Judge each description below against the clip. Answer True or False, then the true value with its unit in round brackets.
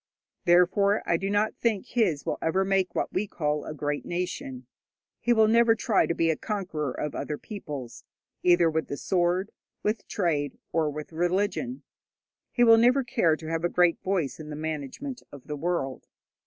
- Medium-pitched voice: True (175 Hz)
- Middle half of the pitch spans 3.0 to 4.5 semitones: False (5.2 semitones)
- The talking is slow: False (180 wpm)